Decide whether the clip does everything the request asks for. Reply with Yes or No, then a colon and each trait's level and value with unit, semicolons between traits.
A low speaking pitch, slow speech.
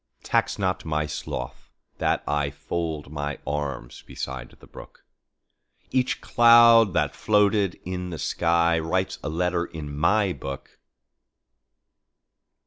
Yes: very low, 85 Hz; slow, 105 wpm